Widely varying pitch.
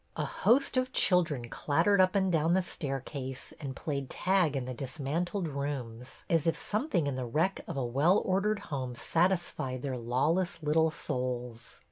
Yes: wide, 5.7 semitones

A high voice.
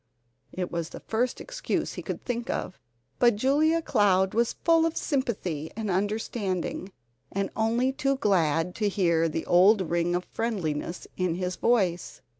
Yes: high, 200 Hz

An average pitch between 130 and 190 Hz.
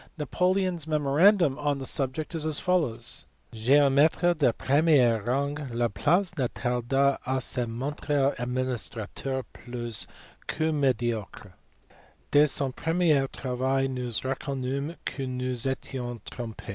Yes: low, 135 Hz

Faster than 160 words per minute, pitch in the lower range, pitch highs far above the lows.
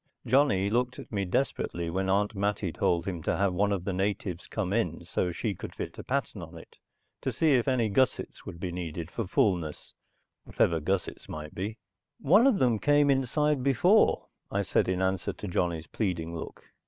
Yes: average, 190 wpm; low, 100 Hz; wide, 5.8 semitones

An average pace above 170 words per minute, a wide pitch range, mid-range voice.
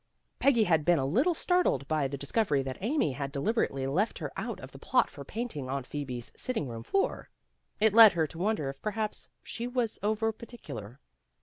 Yes: average, 200 wpm; wide, 8.5 semitones; medium, 175 Hz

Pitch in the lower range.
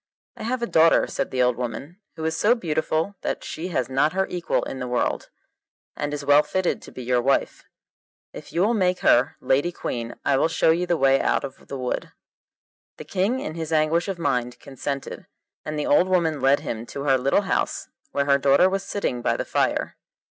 No: medium, 150 Hz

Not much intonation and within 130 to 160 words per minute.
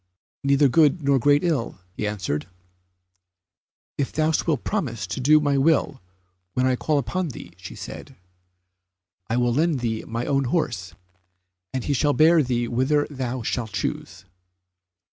No: average, 4.0 semitones; average, 150 wpm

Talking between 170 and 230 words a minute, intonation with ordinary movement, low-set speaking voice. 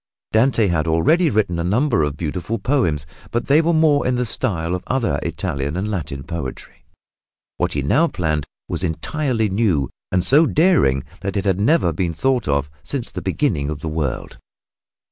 No: average, 180 wpm; wide, 8.6 semitones; very low, 95 Hz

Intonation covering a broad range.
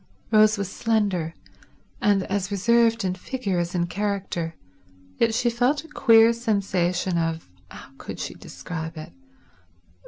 No: average, 4.7 semitones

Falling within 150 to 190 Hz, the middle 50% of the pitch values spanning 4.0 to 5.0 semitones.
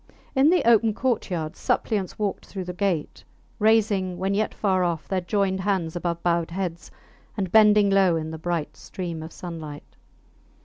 No: medium, 185 Hz; average, 3.3 semitones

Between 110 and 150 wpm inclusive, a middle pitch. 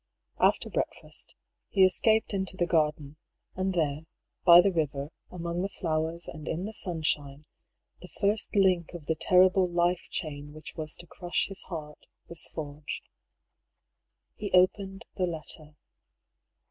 Yes: average, 140 wpm; medium, 170 Hz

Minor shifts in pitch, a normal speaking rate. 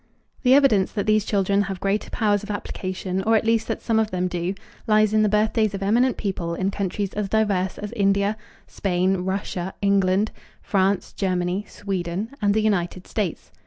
Yes: narrow, 2.3 semitones; average, 180 wpm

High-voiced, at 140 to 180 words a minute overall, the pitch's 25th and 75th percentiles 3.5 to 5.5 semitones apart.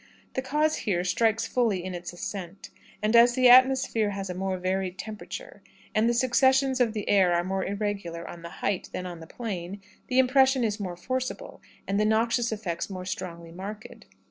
No: high, 205 Hz; average, 190 wpm; average, 4.8 semitones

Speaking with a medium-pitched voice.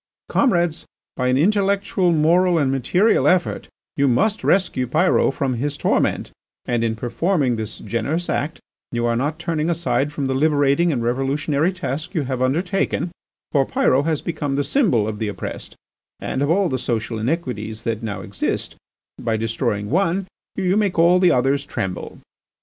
Yes: medium, 145 Hz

